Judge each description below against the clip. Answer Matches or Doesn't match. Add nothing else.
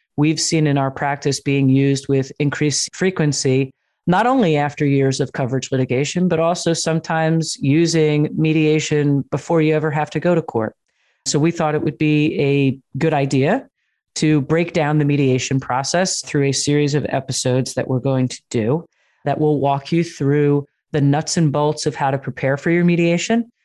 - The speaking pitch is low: Doesn't match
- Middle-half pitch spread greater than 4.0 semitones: Doesn't match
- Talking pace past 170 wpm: Matches